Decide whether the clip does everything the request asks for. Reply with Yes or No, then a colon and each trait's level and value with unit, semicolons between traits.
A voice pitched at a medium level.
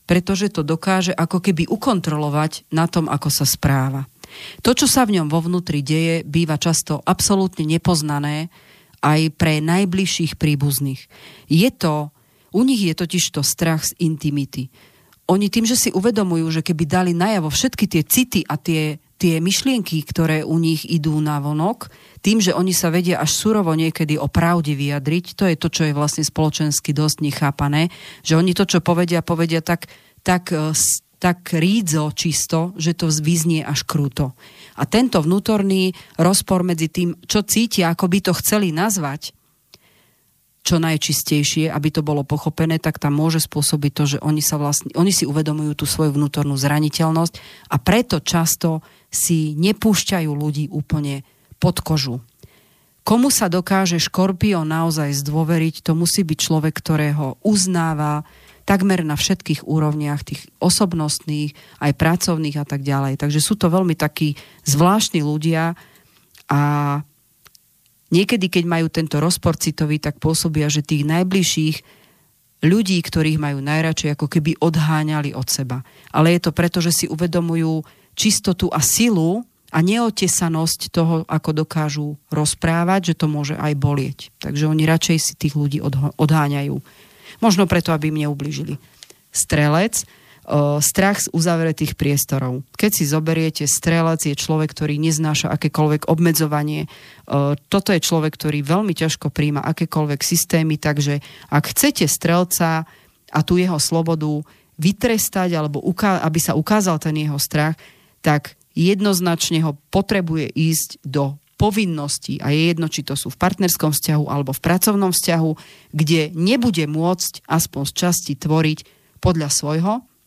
Yes: medium, 160 Hz